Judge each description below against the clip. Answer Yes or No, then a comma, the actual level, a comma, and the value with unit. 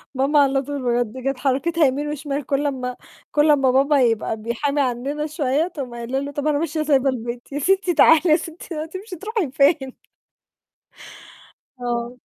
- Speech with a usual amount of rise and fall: Yes, average, 3.0 semitones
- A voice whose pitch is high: Yes, very high, 280 Hz